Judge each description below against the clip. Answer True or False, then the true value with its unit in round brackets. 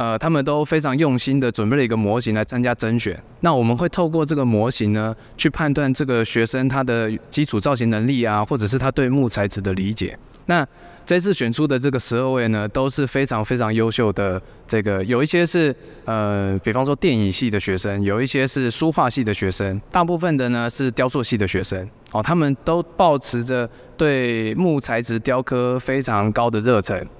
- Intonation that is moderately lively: True (4.2 semitones)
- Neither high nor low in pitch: False (125 Hz)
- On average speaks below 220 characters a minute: False (300 characters per minute)